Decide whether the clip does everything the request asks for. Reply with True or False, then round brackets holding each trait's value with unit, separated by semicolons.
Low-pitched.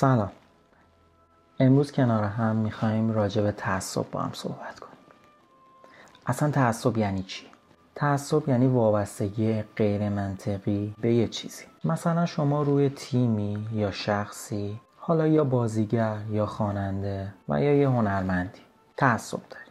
True (110 Hz)